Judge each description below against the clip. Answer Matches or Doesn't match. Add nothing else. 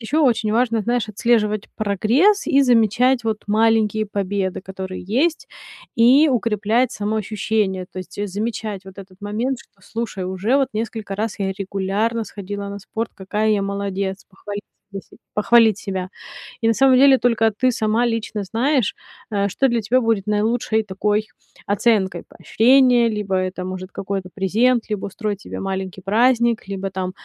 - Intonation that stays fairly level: Doesn't match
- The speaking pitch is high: Matches